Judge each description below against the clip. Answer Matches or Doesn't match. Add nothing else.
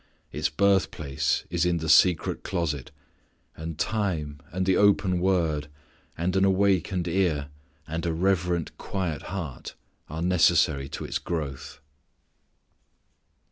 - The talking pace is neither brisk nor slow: Doesn't match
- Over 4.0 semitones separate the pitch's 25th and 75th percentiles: Doesn't match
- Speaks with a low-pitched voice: Matches